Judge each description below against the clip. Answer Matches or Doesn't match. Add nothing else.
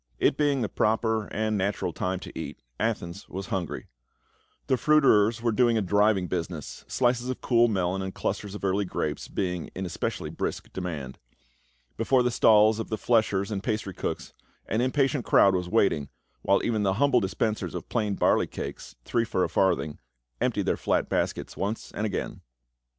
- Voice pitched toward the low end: Matches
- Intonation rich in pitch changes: Doesn't match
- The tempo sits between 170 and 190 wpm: Matches